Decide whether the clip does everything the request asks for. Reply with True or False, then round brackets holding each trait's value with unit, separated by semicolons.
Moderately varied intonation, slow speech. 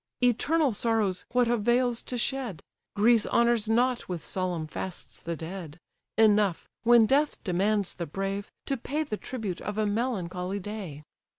False (4.5 semitones; 150 wpm)